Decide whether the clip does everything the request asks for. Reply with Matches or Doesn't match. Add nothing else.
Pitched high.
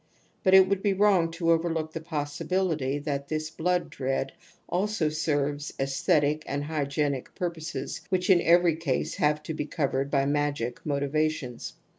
Doesn't match